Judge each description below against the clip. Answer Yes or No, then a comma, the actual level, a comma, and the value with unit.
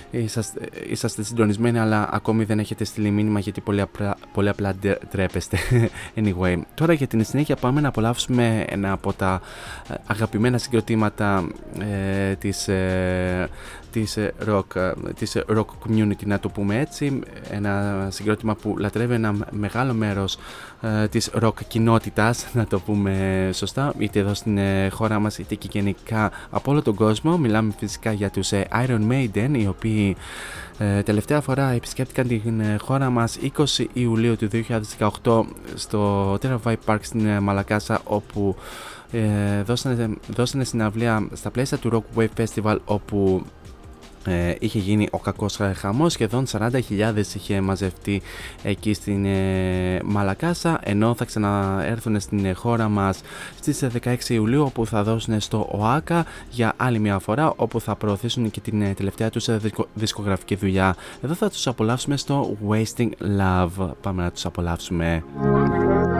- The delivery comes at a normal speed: Yes, average, 140 wpm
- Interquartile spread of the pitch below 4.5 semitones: Yes, average, 2.7 semitones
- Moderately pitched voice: No, low, 105 Hz